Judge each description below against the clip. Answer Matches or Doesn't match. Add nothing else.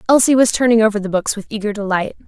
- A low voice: Doesn't match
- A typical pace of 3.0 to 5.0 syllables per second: Doesn't match